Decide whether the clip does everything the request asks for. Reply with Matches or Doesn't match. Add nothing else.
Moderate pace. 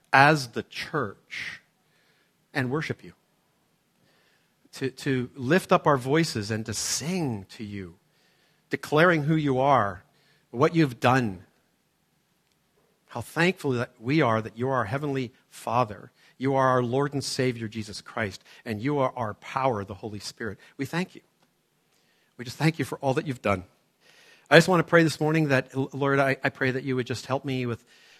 Matches